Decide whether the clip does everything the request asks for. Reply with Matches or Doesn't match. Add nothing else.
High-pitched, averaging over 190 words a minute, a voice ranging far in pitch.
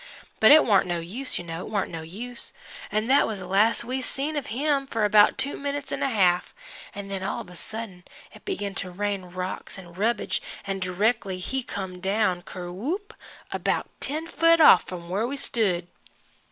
Matches